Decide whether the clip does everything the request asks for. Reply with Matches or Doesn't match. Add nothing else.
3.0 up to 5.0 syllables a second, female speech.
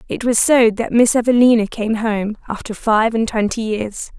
Matches